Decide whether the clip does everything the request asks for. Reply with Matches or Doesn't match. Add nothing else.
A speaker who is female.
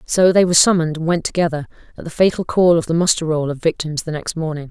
Matches